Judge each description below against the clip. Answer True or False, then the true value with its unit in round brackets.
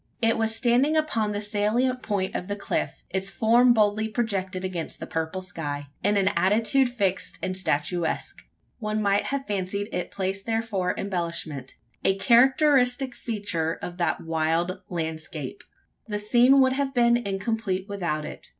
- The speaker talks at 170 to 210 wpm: False (155 wpm)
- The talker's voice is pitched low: False (205 Hz)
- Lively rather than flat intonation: False (4.2 semitones)